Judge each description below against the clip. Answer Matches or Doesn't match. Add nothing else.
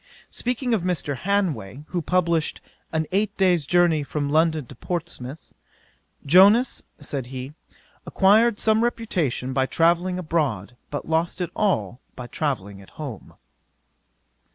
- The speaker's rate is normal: Doesn't match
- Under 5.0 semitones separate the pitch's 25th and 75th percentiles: Doesn't match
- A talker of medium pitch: Matches